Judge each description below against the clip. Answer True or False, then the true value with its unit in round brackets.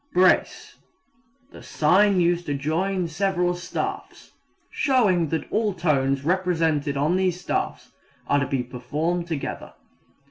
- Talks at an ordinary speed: False (120 wpm)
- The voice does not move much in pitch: False (3.9 semitones)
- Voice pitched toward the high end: False (170 Hz)